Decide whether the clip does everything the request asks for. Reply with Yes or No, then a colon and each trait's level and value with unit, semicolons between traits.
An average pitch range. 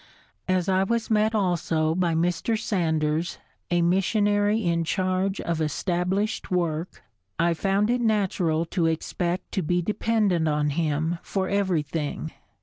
Yes: average, 3.6 semitones